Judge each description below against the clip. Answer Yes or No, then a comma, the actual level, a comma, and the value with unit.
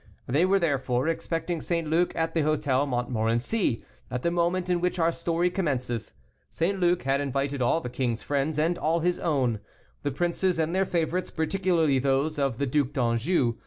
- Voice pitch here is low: No, medium, 155 Hz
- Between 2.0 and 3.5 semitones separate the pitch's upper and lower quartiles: No, average, 4.5 semitones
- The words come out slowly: No, average, 180 wpm